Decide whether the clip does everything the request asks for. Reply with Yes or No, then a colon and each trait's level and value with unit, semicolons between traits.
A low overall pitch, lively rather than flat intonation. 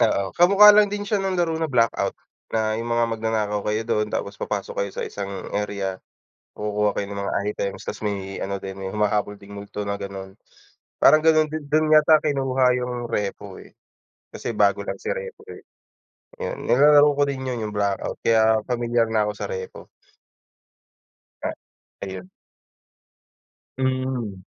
Yes: low, 110 Hz; wide, 5.9 semitones